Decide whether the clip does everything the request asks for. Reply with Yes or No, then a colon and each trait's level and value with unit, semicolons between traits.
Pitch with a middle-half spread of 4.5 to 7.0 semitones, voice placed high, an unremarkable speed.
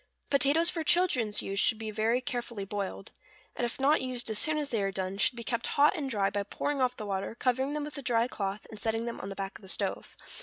No: average, 5.1 semitones; high, 235 Hz; fast, 265 wpm